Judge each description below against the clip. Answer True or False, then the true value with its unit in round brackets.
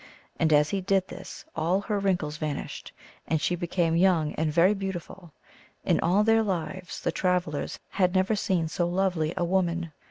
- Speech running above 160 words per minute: True (180 wpm)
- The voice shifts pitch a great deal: False (2.9 semitones)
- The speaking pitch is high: False (180 Hz)